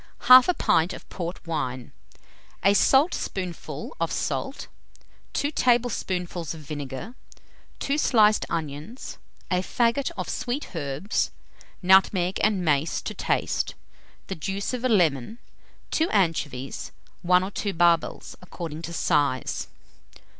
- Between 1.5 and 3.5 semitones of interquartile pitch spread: No, wide, 5.5 semitones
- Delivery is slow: Yes, slow, 120 wpm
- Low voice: No, medium, 180 Hz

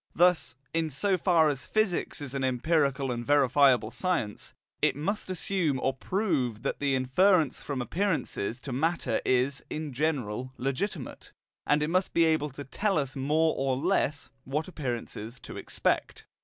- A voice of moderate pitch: Yes, medium, 145 Hz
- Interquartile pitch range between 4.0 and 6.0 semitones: Yes, average, 4.4 semitones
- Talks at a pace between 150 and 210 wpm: Yes, average, 155 wpm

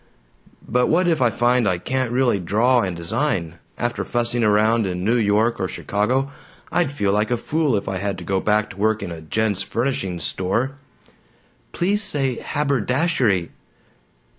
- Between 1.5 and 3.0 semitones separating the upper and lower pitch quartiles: No, average, 4.9 semitones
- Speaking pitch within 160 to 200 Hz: No, low, 115 Hz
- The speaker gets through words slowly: No, average, 165 wpm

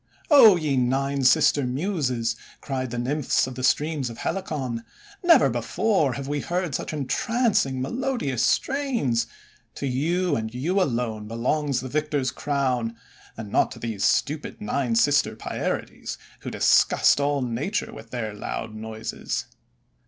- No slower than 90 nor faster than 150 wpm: Yes, average, 145 wpm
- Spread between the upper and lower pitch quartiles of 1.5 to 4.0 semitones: No, average, 4.5 semitones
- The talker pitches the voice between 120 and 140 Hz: Yes, low, 135 Hz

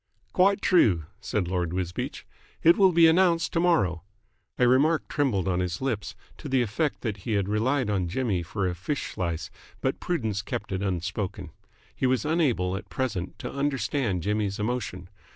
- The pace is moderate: Yes, average, 170 wpm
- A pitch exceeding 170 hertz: No, low, 105 Hz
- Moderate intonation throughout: No, wide, 7.5 semitones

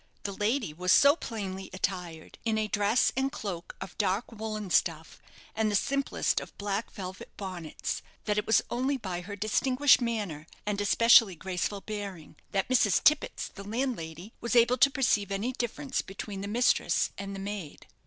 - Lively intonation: No, average, 3.7 semitones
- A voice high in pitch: Yes, high, 205 Hz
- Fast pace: No, average, 170 wpm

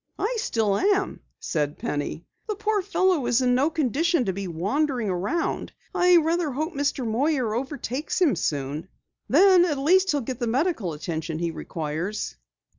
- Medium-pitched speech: No, very high, 265 Hz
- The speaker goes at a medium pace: Yes, average, 160 wpm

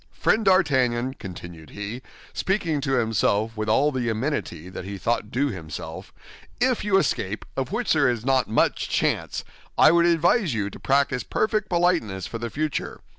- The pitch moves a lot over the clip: Yes, wide, 7.5 semitones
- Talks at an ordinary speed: Yes, average, 170 wpm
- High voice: No, low, 130 Hz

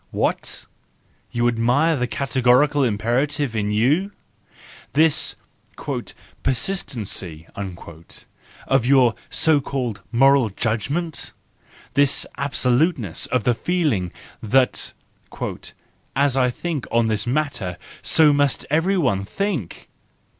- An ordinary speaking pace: No, slow, 105 wpm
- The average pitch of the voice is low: Yes, low, 130 Hz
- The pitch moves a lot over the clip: No, average, 4.4 semitones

